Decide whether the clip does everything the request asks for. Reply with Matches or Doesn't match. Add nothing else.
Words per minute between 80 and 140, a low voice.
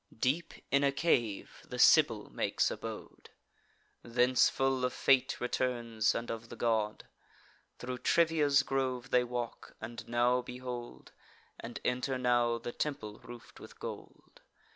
Matches